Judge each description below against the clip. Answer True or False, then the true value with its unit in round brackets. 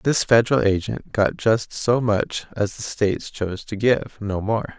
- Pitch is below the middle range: True (110 Hz)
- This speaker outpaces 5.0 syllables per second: False (4.5 syllables/s)